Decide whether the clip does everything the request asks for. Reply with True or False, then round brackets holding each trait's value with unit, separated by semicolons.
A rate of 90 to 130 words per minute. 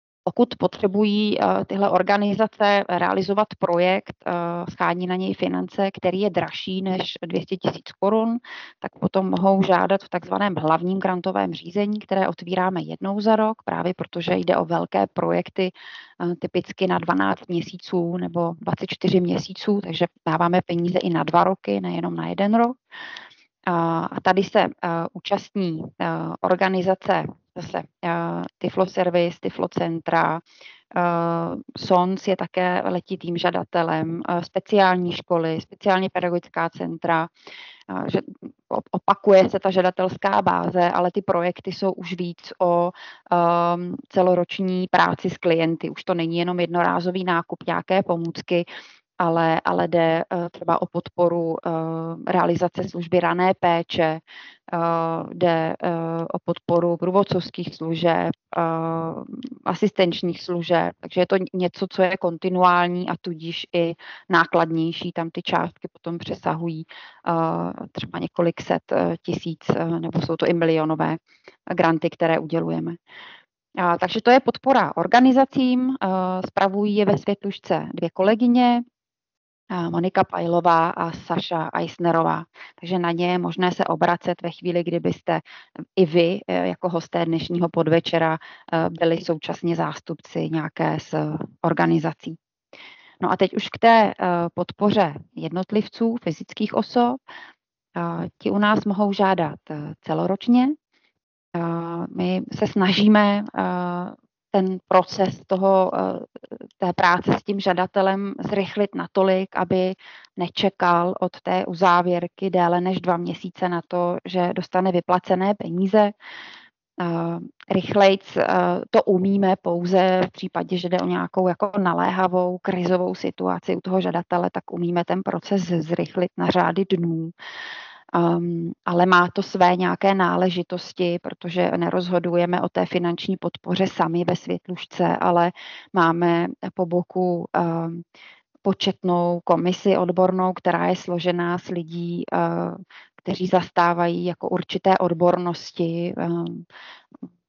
True (125 wpm)